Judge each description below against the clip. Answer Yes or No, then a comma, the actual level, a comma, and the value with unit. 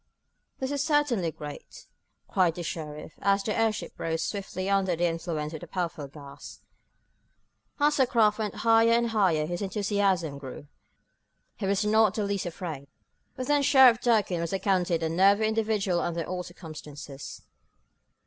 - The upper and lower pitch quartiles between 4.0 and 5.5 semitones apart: Yes, average, 4.9 semitones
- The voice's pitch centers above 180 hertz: Yes, high, 190 Hz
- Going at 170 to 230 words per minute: No, average, 155 wpm